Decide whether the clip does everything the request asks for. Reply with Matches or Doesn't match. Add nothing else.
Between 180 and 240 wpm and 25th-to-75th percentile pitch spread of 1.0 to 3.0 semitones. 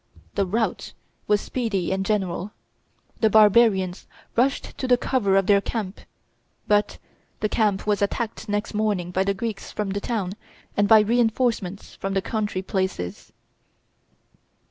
Doesn't match